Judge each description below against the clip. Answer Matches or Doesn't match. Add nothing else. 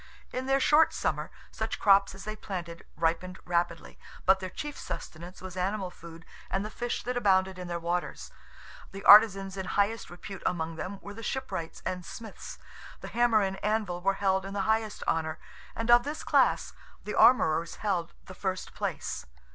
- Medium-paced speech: Matches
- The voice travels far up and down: Doesn't match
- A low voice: Doesn't match